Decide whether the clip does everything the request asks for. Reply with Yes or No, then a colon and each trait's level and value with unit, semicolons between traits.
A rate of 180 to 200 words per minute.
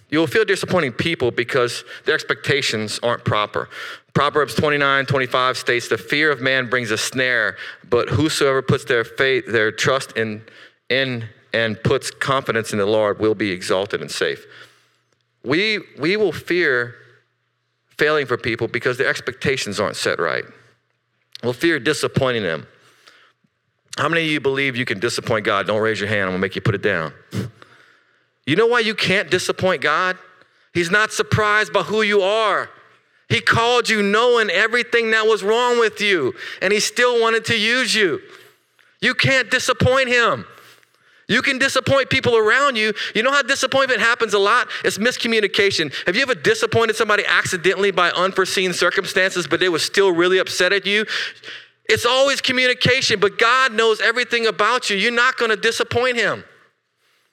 No: average, 170 wpm